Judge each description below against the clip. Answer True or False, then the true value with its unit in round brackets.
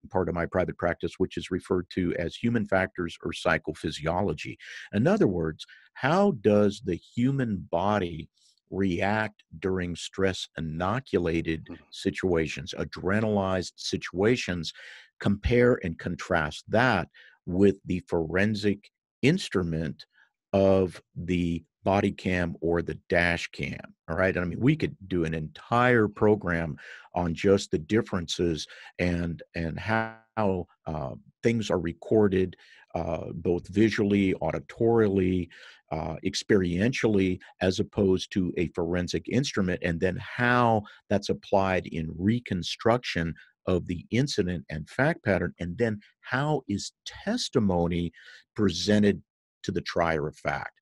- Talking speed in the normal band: False (120 wpm)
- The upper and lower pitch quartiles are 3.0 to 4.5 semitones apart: True (3.6 semitones)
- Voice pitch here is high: False (95 Hz)